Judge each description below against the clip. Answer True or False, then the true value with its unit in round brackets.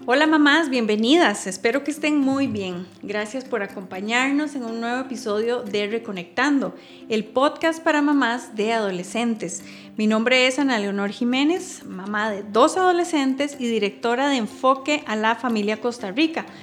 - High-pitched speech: True (240 Hz)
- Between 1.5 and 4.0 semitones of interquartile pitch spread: False (5.1 semitones)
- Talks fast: False (150 wpm)